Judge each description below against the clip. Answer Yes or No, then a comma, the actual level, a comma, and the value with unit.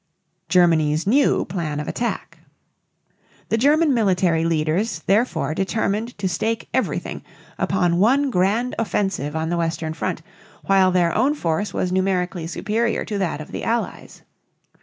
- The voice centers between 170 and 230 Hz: Yes, high, 190 Hz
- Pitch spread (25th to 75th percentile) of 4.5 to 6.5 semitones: Yes, average, 5.2 semitones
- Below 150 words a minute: Yes, average, 140 wpm